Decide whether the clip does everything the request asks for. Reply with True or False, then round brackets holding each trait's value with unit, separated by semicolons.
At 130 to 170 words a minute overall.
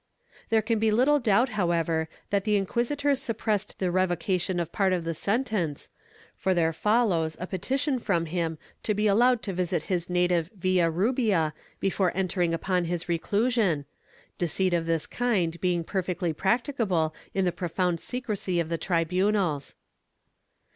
True (150 wpm)